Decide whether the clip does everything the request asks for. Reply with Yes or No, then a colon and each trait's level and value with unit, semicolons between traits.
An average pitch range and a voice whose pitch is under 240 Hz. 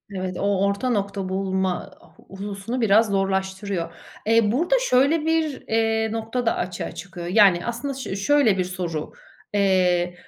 Yes: average, 3.3 semitones; high, 200 Hz